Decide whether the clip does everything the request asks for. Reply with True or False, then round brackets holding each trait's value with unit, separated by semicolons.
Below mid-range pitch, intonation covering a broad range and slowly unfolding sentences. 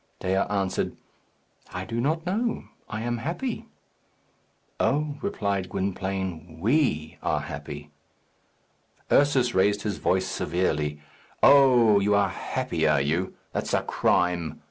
True (100 Hz; 6.8 semitones; 120 wpm)